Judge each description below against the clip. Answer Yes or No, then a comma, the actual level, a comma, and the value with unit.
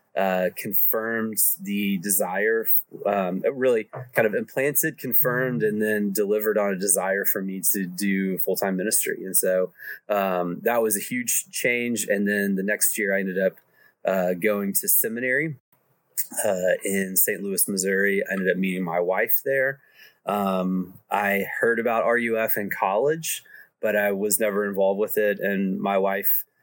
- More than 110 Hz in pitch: No, low, 105 Hz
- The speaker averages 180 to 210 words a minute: No, average, 160 wpm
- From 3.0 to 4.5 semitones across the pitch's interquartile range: Yes, average, 3.3 semitones